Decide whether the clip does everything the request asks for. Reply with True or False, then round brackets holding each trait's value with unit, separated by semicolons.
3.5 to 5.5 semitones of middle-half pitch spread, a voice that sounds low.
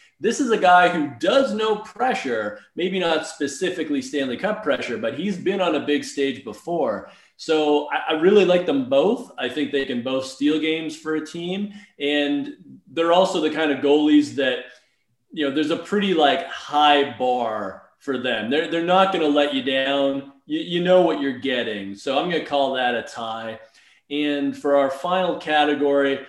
False (4.3 semitones; 150 Hz)